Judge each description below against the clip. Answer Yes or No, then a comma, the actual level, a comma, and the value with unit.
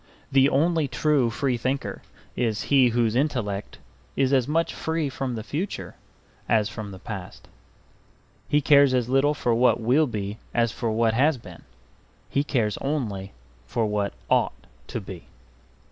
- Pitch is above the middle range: No, low, 125 Hz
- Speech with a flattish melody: No, average, 4.4 semitones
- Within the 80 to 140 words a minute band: No, average, 155 wpm